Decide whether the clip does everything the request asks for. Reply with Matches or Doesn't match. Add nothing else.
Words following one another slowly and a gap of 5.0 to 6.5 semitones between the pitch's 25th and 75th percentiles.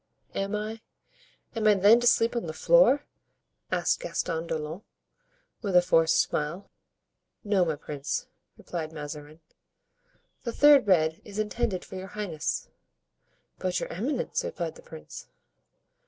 Matches